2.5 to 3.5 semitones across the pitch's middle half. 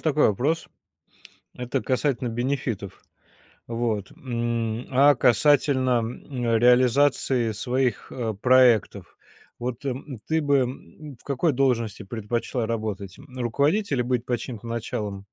Yes: average, 2.9 semitones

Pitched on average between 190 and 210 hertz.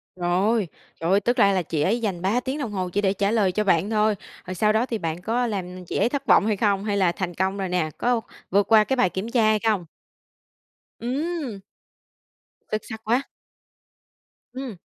Yes: high, 205 Hz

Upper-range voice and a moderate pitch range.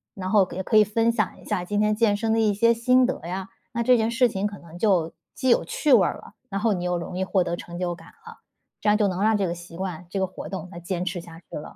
Yes: high, 195 Hz; average, 3.7 semitones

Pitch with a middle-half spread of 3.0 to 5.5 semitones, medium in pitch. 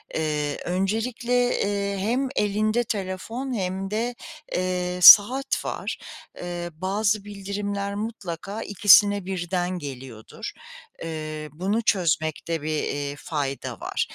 No: average, 4.0 semitones; high, 195 Hz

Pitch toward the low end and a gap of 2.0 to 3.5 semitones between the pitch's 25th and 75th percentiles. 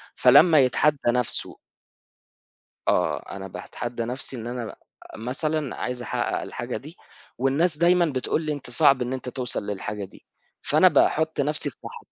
No: low, 130 Hz; average, 3.9 semitones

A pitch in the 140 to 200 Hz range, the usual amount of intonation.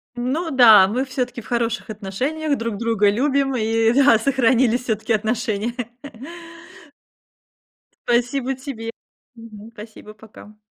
No: high, 235 Hz; average, 3.0 semitones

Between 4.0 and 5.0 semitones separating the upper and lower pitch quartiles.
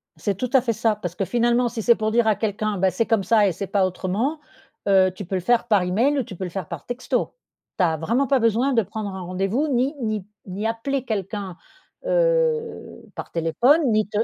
Yes: average, 4.3 semitones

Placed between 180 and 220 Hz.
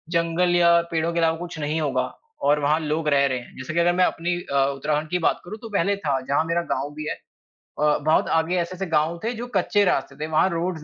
No: medium, 160 Hz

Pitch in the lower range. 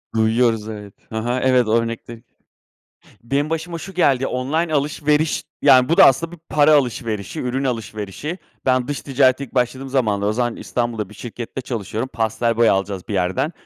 Yes: low, 125 Hz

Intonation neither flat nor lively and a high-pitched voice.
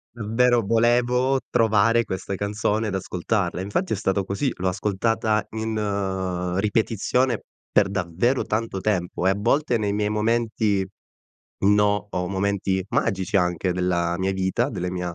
No: average, 3.0 semitones; low, 100 Hz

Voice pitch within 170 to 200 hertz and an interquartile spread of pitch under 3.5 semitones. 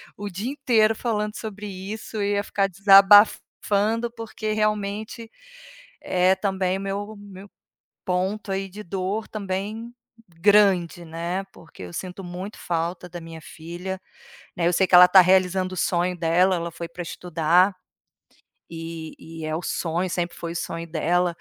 Yes: medium, 185 Hz; average, 2.9 semitones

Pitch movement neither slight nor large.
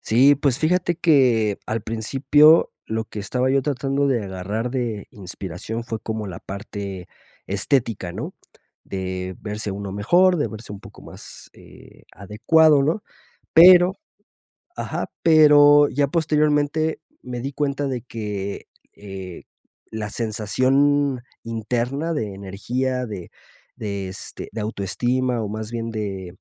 No: wide, 5.7 semitones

